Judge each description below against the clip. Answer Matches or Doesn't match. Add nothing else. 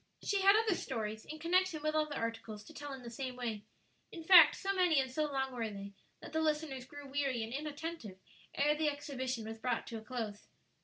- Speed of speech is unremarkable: Doesn't match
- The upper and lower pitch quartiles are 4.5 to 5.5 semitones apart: Matches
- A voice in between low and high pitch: Doesn't match